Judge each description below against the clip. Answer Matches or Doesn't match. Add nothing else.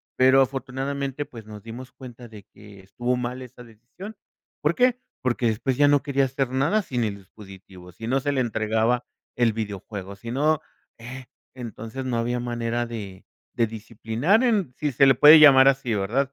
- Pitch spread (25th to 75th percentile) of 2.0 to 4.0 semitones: Matches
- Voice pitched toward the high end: Doesn't match